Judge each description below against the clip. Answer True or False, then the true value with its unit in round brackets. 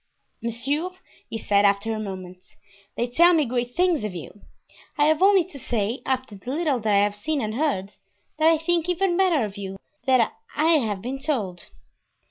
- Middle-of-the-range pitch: False (245 Hz)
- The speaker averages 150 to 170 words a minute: False (190 wpm)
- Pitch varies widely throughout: True (7.2 semitones)